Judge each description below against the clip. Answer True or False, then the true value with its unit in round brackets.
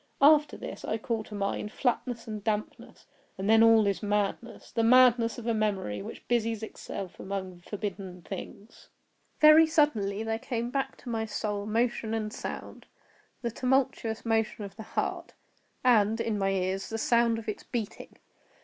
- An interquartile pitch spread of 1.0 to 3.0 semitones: True (2.4 semitones)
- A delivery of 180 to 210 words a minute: False (160 wpm)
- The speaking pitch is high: True (220 Hz)